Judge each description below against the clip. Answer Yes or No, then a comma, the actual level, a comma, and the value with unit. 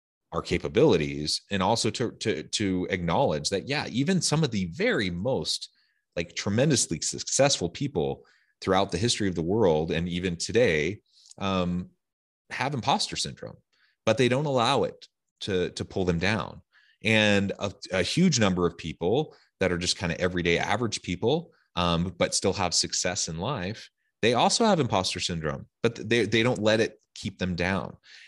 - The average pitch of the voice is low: Yes, very low, 95 Hz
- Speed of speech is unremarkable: Yes, average, 170 wpm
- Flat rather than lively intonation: No, average, 4.2 semitones